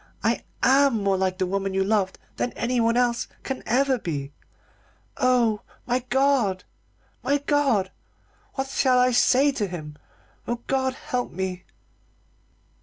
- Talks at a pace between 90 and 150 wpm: Yes, slow, 135 wpm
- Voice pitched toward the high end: Yes, high, 240 Hz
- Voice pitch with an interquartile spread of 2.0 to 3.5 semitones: No, wide, 5.4 semitones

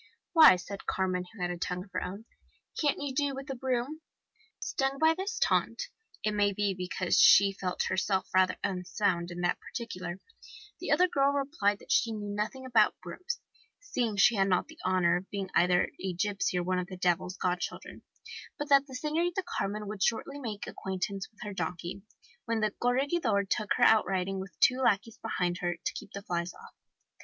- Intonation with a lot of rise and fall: Yes, wide, 6.0 semitones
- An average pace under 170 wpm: No, average, 195 wpm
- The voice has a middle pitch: No, high, 200 Hz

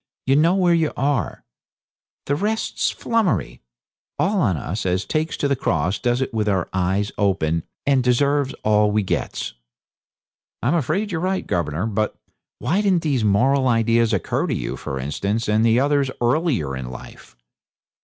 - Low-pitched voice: Yes, low, 120 Hz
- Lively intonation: Yes, wide, 7.1 semitones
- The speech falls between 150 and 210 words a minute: Yes, average, 160 wpm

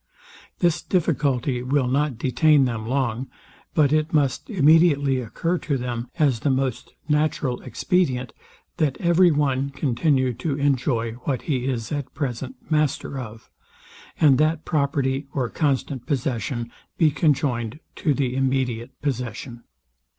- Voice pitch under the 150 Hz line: Yes, low, 135 Hz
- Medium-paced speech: No, slow, 130 wpm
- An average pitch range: Yes, average, 3.2 semitones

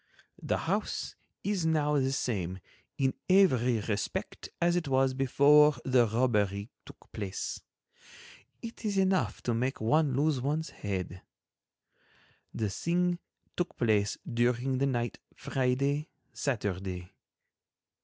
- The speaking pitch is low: Yes, low, 130 Hz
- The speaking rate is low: Yes, slow, 115 wpm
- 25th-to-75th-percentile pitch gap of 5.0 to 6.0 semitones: Yes, wide, 5.5 semitones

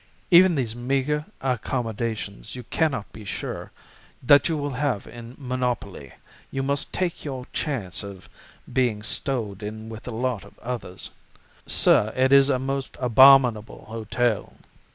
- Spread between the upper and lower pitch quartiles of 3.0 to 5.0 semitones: Yes, average, 3.8 semitones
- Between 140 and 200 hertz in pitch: No, low, 125 Hz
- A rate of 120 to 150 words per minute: Yes, average, 140 wpm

